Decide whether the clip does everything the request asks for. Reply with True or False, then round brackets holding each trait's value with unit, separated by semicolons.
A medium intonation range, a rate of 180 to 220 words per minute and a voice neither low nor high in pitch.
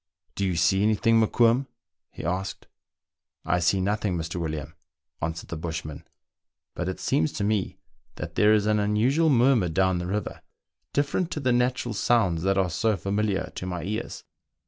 False (4.4 semitones; 185 wpm; 100 Hz)